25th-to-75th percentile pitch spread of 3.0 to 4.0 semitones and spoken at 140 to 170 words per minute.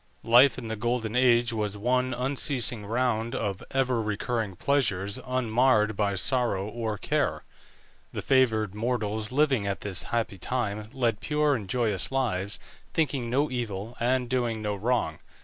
Yes: average, 3.3 semitones; average, 150 wpm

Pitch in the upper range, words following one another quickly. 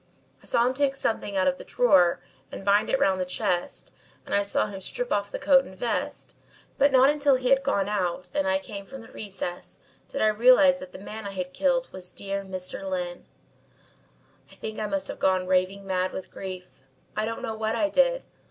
Yes: high, 210 Hz; fast, 215 wpm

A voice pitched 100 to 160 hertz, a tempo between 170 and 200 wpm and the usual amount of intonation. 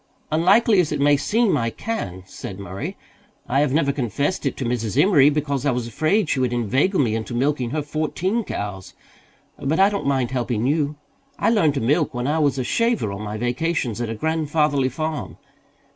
Yes: medium, 140 Hz; average, 195 wpm; average, 4.7 semitones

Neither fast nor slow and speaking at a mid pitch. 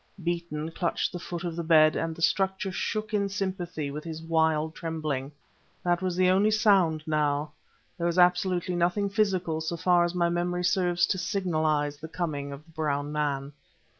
Yes: average, 180 wpm; medium, 170 Hz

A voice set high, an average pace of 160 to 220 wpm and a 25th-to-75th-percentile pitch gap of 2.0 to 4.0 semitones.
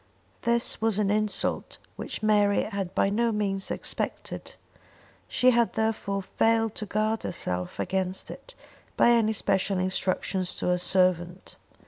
No: high, 205 Hz; slow, 135 wpm; average, 2.9 semitones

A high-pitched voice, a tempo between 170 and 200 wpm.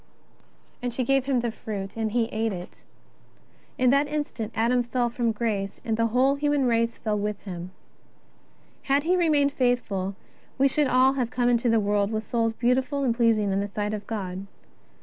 Yes: high, 235 Hz; average, 190 wpm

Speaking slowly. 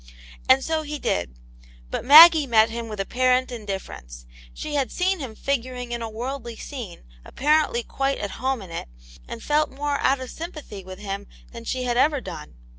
No: average, 185 wpm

